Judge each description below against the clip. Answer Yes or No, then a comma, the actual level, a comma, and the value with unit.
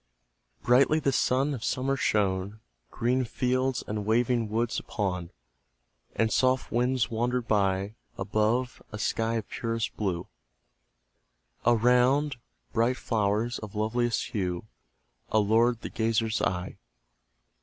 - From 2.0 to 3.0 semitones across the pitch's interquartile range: Yes, average, 2.7 semitones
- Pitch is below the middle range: Yes, low, 115 Hz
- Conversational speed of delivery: No, slow, 110 wpm